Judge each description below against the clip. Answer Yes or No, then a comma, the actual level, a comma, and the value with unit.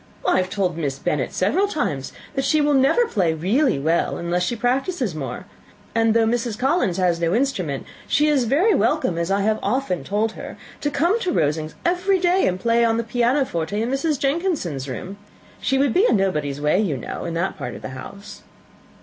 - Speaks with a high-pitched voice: Yes, high, 220 Hz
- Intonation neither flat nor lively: No, wide, 8.4 semitones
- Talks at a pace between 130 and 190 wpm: No, average, 200 wpm